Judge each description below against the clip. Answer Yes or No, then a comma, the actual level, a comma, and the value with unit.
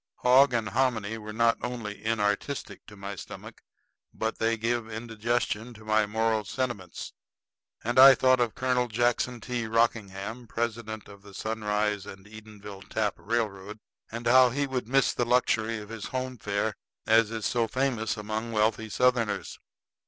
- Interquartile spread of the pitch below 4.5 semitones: Yes, narrow, 2.4 semitones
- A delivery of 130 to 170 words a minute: Yes, average, 155 wpm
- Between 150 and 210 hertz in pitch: No, low, 110 Hz